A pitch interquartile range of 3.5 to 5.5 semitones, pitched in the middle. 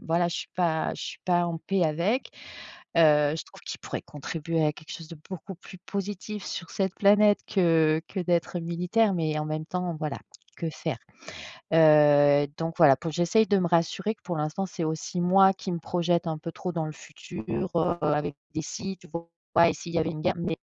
No: average, 2.7 semitones; medium, 170 Hz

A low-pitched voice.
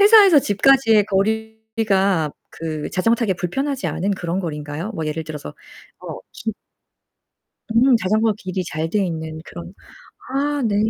No: high, 200 Hz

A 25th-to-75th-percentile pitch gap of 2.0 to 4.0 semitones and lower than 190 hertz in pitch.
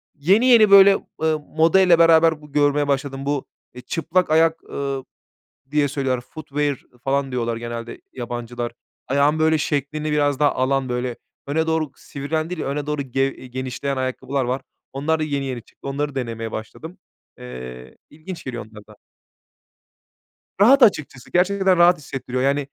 Yes: average, 3.6 semitones; medium, 140 Hz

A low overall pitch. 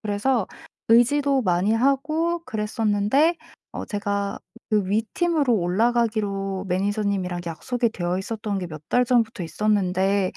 No: high, 210 Hz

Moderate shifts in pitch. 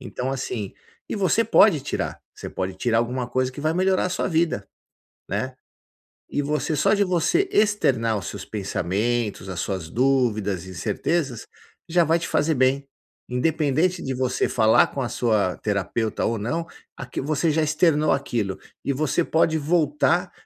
No: wide, 6.2 semitones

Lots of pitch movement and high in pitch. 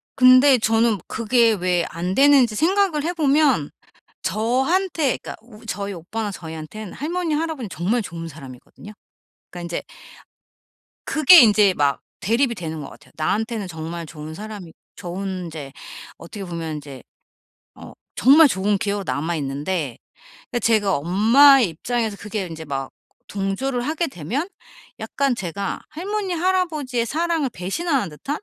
Yes: wide, 8.0 semitones; high, 215 Hz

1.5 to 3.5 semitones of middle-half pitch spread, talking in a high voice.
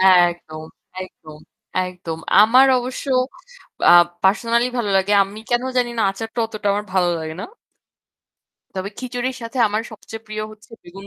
No: average, 4.0 semitones; high, 215 Hz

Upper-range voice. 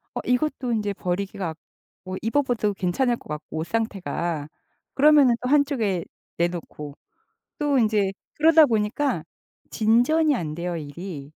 Yes: high, 215 Hz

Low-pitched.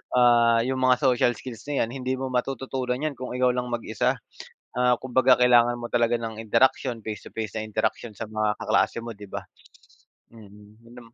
Yes: low, 120 Hz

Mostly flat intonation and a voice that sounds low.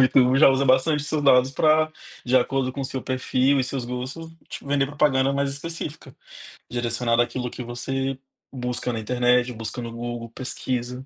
Yes: narrow, 2.0 semitones; low, 130 Hz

